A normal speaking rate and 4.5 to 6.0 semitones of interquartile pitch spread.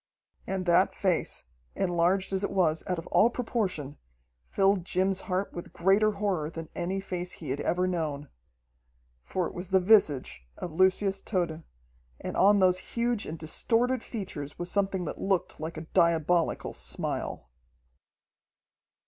No: average, 150 wpm; average, 2.9 semitones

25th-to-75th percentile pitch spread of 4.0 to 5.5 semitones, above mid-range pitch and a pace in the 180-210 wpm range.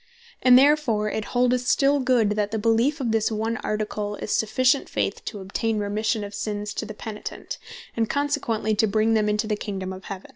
No: average, 2.8 semitones; high, 220 Hz; average, 195 wpm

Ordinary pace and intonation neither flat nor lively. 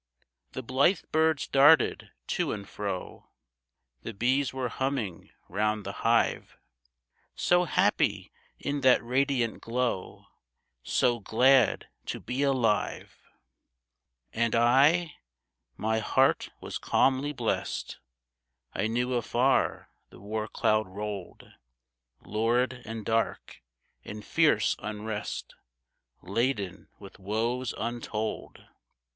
No: slow, 100 wpm; average, 3.6 semitones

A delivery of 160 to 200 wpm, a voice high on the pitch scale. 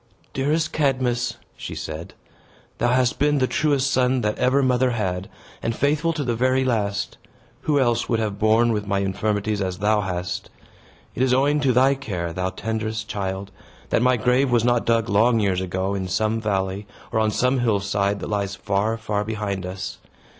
No: average, 180 wpm; low, 110 Hz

